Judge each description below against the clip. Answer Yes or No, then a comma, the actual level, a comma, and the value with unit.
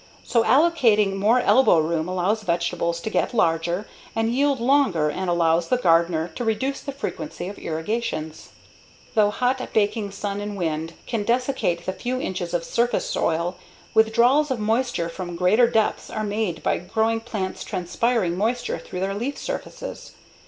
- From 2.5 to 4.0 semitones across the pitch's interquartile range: No, wide, 5.5 semitones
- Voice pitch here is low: No, high, 210 Hz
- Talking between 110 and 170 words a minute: Yes, average, 160 wpm